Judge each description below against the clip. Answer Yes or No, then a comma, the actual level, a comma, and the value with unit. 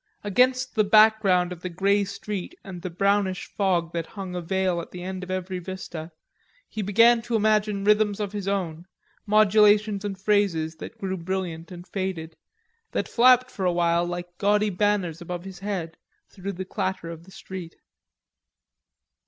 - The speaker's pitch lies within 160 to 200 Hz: Yes, high, 190 Hz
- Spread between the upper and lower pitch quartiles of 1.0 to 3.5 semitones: Yes, average, 2.8 semitones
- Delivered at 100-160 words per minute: No, average, 170 wpm